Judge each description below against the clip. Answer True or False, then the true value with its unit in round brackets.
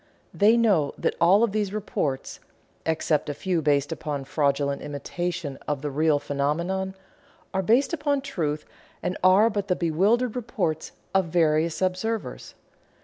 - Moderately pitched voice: True (175 Hz)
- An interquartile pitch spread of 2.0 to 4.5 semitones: False (5.5 semitones)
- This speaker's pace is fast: False (145 wpm)